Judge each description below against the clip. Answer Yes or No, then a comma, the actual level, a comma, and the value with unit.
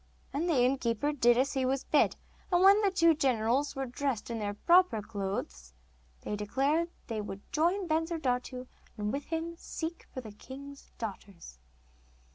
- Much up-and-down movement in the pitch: Yes, wide, 6.6 semitones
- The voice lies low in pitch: No, very high, 265 Hz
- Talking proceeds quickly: No, average, 160 wpm